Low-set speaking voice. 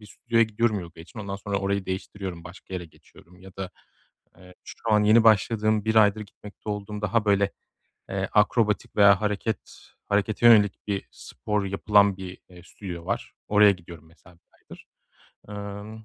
Yes: low, 100 Hz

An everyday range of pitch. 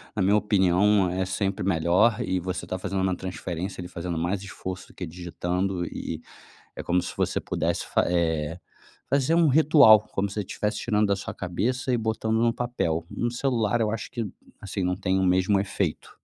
Yes: average, 3.2 semitones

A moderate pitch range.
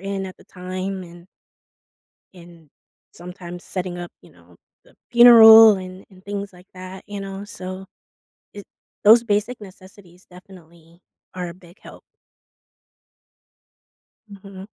No: narrow, 2.0 semitones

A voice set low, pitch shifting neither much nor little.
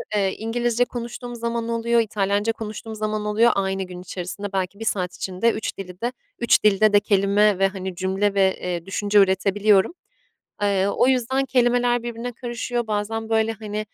No: high, 210 Hz; average, 3.1 semitones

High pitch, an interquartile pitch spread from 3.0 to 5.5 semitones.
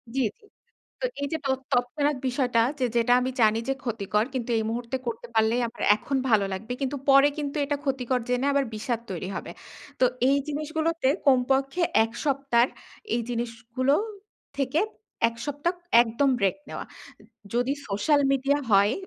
Yes: very high, 255 Hz; average, 3.3 semitones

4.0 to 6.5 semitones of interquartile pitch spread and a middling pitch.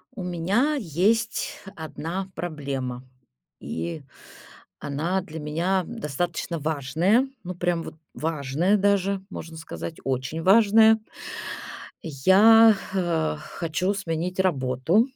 Yes: average, 4.3 semitones; medium, 175 Hz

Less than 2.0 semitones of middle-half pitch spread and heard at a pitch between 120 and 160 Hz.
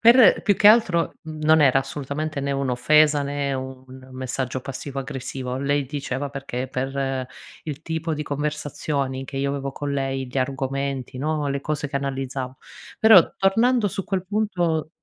No: average, 2.7 semitones; medium, 140 Hz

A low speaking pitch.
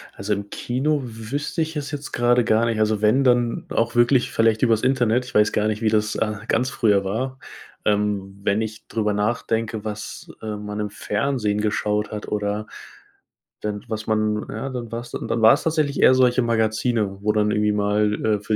Yes: low, 110 Hz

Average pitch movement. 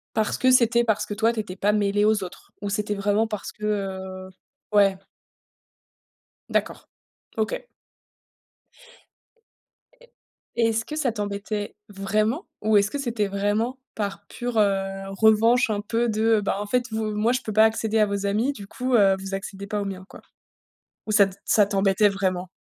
No: narrow, 2.0 semitones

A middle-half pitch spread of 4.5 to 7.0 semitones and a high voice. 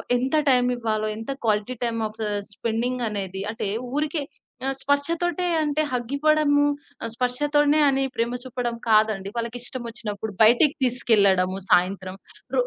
Yes: average, 4.8 semitones; high, 240 Hz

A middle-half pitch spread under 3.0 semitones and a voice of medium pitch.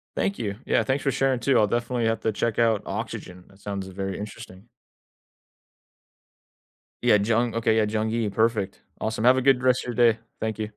No: narrow, 2.6 semitones; low, 110 Hz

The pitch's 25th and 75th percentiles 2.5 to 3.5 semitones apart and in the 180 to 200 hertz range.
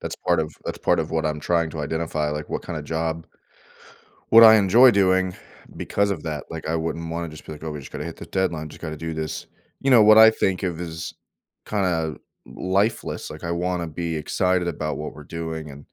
No: average, 3.0 semitones; very low, 85 Hz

